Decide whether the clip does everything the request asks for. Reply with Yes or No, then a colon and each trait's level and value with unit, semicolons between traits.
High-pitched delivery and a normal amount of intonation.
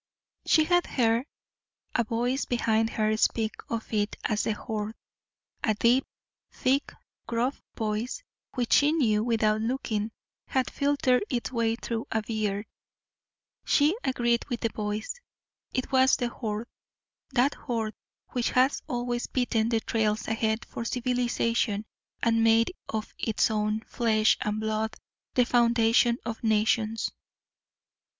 No: high, 230 Hz; narrow, 2.2 semitones